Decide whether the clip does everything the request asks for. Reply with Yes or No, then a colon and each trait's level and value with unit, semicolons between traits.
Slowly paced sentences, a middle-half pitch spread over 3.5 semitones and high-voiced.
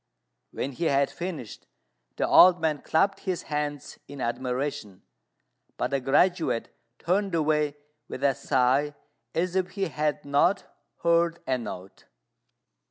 No: slow, 130 wpm; average, 4.0 semitones; medium, 150 Hz